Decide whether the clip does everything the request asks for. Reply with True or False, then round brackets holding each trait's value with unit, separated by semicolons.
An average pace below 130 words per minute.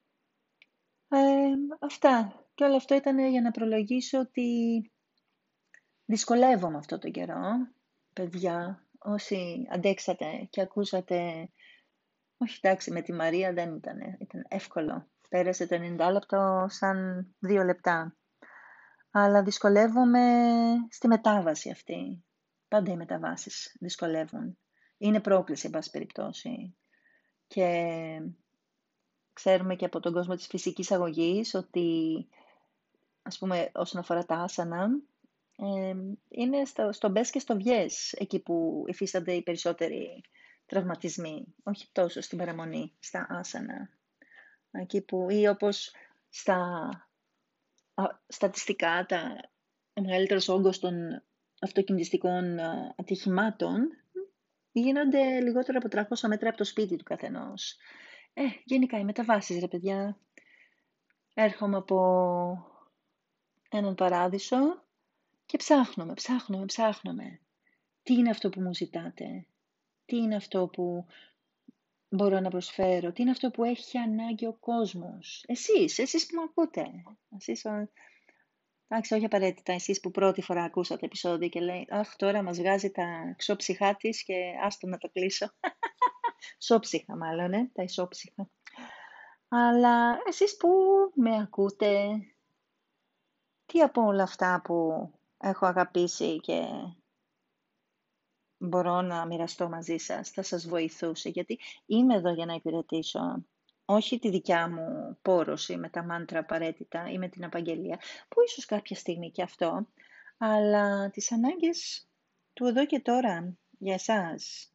True (120 wpm)